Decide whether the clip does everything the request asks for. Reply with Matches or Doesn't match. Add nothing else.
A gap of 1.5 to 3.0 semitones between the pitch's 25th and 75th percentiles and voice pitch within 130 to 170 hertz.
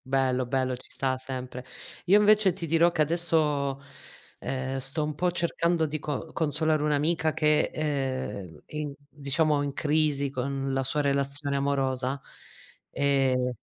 Matches